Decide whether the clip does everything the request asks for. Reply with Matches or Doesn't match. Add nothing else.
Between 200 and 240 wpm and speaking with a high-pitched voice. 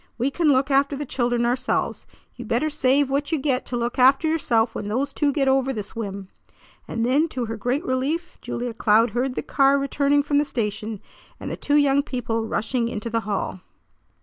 Matches